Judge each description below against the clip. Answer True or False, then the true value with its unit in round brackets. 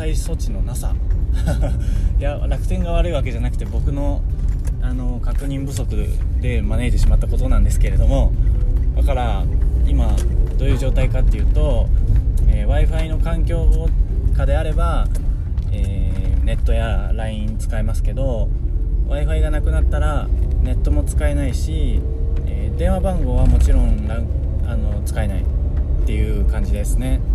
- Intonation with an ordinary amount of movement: True (3.9 semitones)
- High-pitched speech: False (75 Hz)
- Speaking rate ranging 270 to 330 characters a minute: True (295 characters per minute)